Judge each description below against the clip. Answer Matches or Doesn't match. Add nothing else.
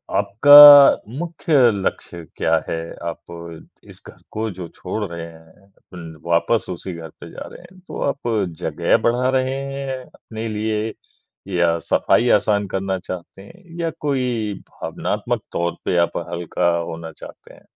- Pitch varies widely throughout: Matches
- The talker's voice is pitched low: Matches